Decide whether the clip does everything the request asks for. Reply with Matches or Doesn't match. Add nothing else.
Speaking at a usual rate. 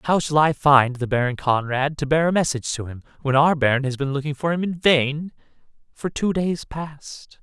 Doesn't match